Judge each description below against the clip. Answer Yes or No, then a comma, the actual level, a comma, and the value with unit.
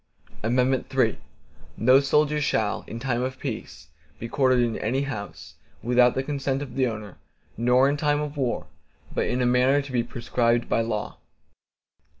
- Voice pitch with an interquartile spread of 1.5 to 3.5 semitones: Yes, average, 2.7 semitones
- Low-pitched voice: Yes, low, 125 Hz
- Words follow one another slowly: No, average, 160 wpm